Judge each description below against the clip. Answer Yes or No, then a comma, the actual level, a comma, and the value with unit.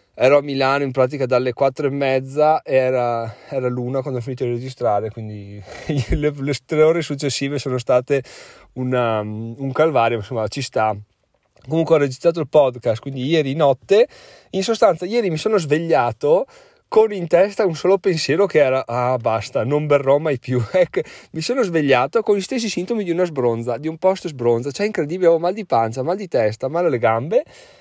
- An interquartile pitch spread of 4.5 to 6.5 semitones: Yes, wide, 5.5 semitones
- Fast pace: Yes, fast, 185 wpm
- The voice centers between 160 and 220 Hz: No, medium, 140 Hz